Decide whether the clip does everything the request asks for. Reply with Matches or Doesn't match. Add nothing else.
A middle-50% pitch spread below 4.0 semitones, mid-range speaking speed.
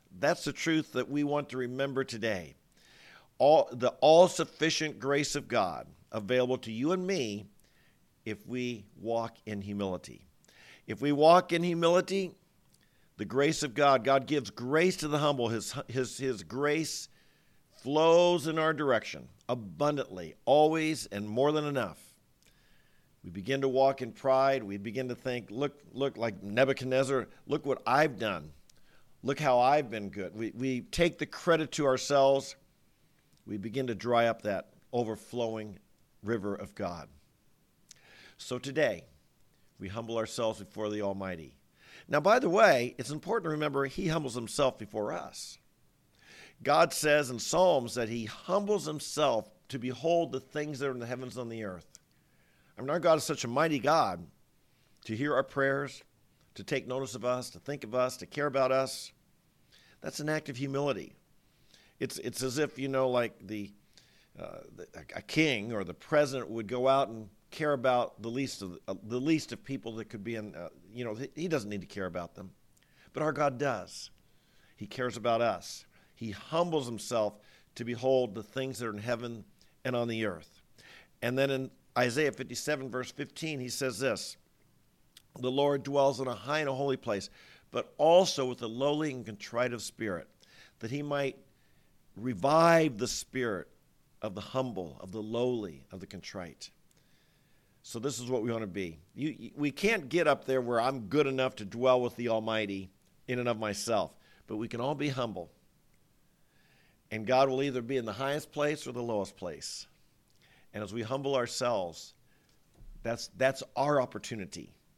Doesn't match